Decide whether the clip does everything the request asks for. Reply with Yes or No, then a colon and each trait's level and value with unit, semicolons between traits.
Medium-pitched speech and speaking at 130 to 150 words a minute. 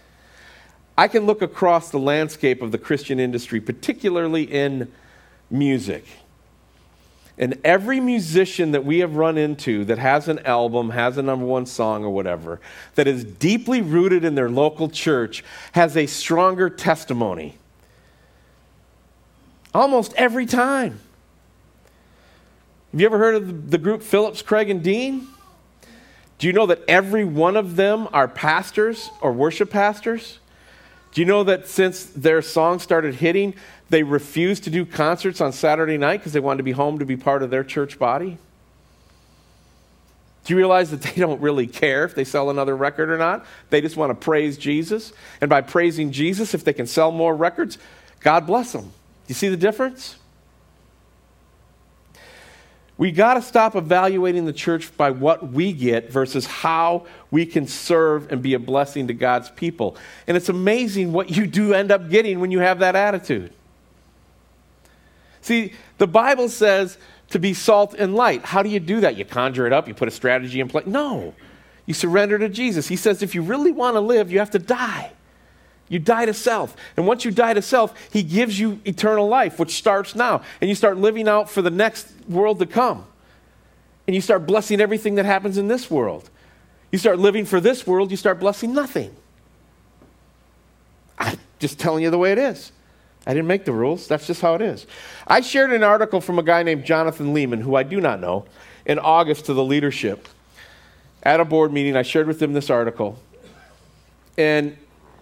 No: medium, 170 Hz; average, 180 wpm